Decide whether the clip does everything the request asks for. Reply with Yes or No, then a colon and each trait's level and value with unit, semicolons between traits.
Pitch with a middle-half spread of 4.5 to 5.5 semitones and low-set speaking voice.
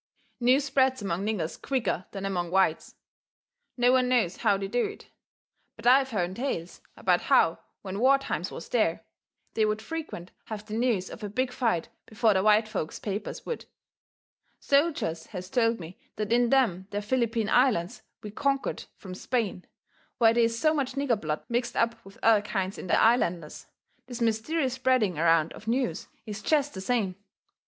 No: average, 4.8 semitones; high, 225 Hz